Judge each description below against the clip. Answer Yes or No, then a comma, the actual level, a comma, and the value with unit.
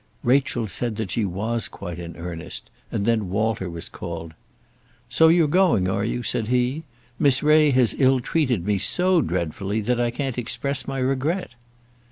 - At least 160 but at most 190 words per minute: Yes, average, 170 wpm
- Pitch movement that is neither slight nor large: No, wide, 5.9 semitones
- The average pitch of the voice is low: Yes, low, 120 Hz